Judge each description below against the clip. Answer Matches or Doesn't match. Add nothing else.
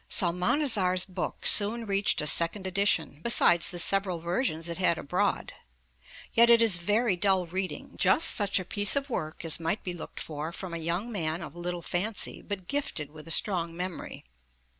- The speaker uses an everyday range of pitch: Matches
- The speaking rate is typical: Matches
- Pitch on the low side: Doesn't match